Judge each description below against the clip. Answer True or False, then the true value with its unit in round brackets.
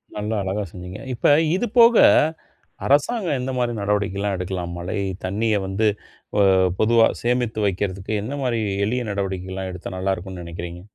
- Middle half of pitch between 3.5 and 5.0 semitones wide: True (3.8 semitones)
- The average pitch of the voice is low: True (100 Hz)